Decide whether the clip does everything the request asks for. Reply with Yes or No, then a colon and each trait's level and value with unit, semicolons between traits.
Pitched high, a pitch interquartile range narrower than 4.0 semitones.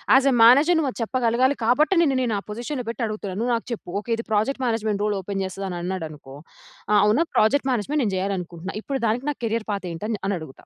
No: high, 220 Hz; average, 4.6 semitones